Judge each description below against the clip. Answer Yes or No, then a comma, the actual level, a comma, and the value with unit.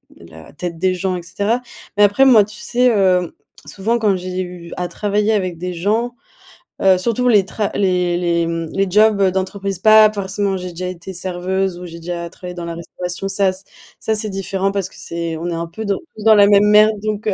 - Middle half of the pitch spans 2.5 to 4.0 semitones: Yes, average, 2.8 semitones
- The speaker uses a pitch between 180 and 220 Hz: Yes, high, 190 Hz